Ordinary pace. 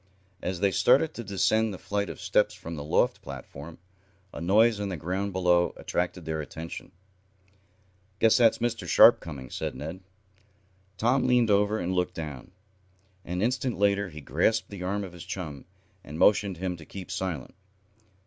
Yes: average, 170 wpm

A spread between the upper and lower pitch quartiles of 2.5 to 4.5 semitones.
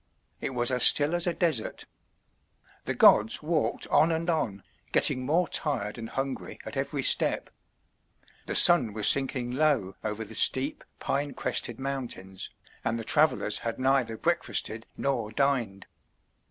No: average, 4.9 semitones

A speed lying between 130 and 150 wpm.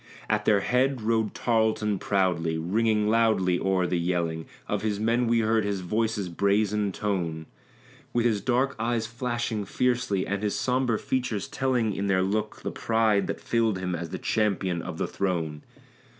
No: average, 165 wpm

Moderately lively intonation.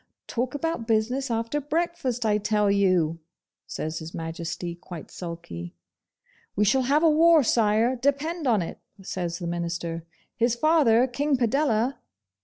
No: wide, 7.9 semitones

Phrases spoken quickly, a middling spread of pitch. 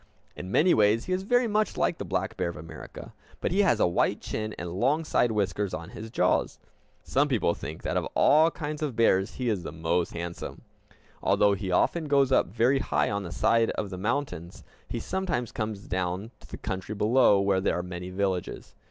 No: fast, 210 wpm; wide, 6.8 semitones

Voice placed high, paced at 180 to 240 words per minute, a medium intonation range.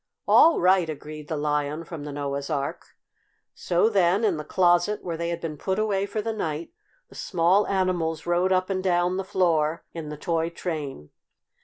No: medium, 170 Hz; average, 185 wpm; average, 3.6 semitones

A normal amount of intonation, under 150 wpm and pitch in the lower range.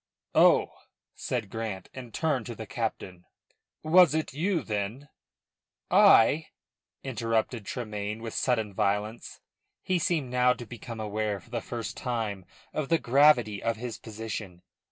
Yes: average, 3.6 semitones; average, 140 wpm; low, 115 Hz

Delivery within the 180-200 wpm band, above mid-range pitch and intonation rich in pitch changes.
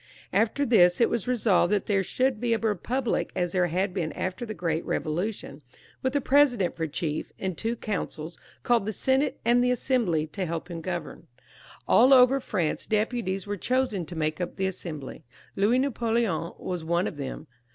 Yes: average, 185 wpm; high, 195 Hz; wide, 5.8 semitones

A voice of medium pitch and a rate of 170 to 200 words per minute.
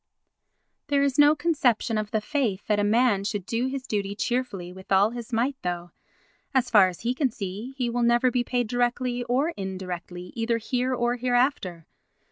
No: high, 235 Hz; average, 185 wpm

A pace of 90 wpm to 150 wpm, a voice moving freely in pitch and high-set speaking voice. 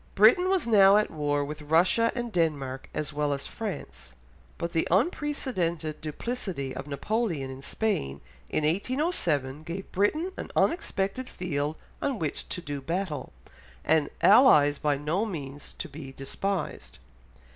No: average, 140 wpm; wide, 6.7 semitones; medium, 165 Hz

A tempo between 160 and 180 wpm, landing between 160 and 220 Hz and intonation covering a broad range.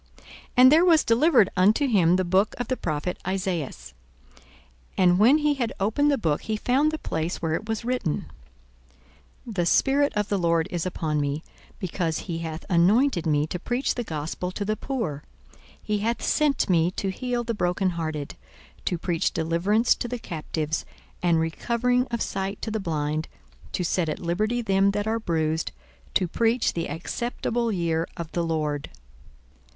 Yes: average, 175 wpm; high, 190 Hz; wide, 6.1 semitones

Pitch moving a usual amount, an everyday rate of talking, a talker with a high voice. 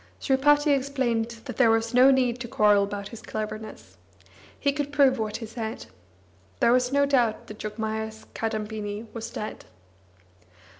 Yes: average, 3.4 semitones; average, 150 wpm; high, 230 Hz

